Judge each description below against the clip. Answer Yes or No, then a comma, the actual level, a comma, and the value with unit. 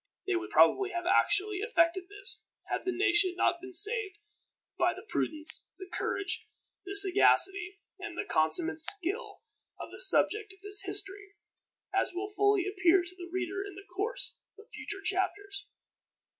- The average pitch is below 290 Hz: No, very high, 390 Hz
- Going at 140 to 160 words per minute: Yes, average, 155 wpm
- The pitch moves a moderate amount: No, narrow, 1.9 semitones